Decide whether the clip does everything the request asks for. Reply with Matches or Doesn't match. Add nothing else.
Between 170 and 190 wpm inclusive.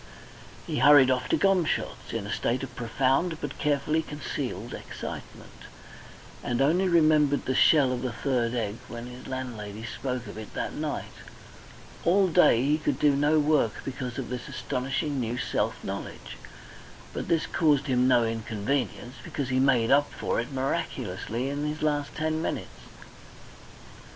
Doesn't match